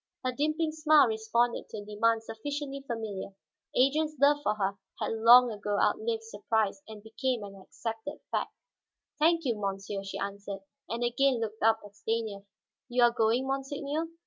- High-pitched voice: Yes, high, 230 Hz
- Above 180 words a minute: No, average, 160 wpm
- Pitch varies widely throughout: No, average, 4.5 semitones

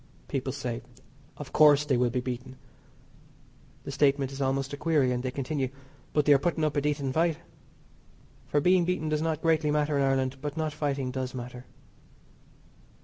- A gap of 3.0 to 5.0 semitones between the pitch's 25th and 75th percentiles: No, narrow, 2.6 semitones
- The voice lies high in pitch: No, medium, 140 Hz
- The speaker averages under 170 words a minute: No, average, 180 wpm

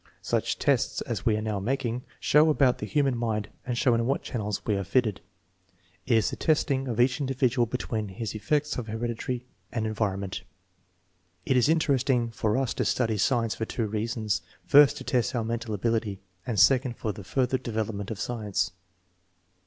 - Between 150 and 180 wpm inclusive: No, average, 190 wpm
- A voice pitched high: No, low, 115 Hz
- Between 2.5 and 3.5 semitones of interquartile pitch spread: Yes, average, 3.2 semitones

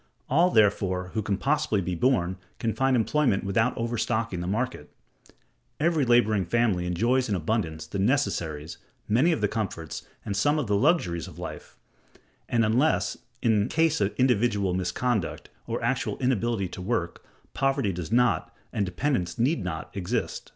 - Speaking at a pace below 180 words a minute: Yes, average, 155 wpm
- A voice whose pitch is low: Yes, low, 110 Hz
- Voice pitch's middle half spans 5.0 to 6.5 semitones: Yes, wide, 5.5 semitones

